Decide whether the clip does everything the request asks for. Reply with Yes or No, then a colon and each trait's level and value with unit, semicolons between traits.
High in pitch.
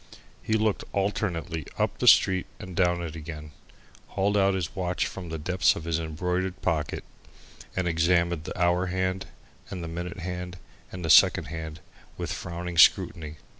No: very low, 90 Hz